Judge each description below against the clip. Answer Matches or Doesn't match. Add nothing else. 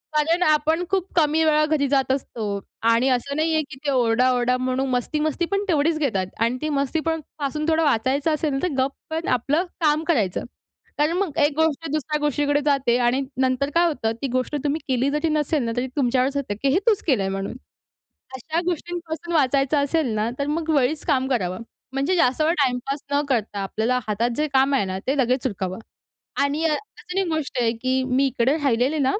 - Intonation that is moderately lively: Matches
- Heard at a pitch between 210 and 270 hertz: Doesn't match